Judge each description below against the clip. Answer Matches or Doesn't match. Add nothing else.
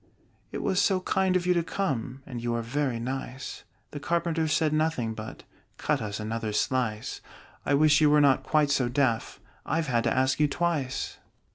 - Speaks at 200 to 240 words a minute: Doesn't match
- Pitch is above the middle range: Doesn't match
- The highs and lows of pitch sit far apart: Doesn't match